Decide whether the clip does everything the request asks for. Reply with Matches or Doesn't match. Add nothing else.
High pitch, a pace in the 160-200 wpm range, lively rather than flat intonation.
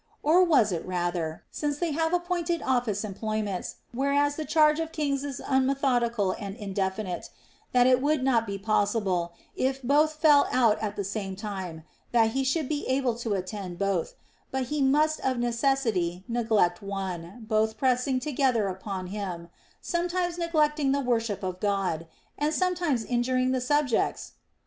Matches